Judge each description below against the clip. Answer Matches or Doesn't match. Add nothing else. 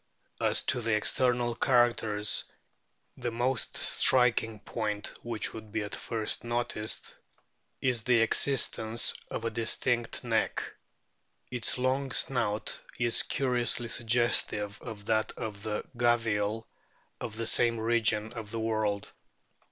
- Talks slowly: Matches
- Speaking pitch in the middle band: Doesn't match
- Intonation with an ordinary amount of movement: Doesn't match